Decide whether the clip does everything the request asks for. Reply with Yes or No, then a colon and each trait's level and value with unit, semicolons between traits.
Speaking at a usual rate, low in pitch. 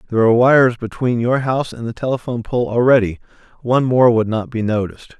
Yes: average, 185 wpm; low, 120 Hz